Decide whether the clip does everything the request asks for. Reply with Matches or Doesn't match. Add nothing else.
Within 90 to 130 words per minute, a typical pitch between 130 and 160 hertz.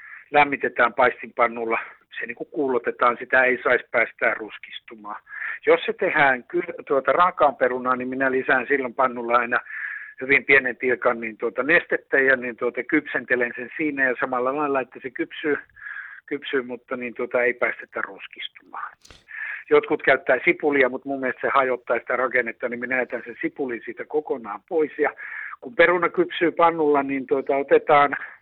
Doesn't match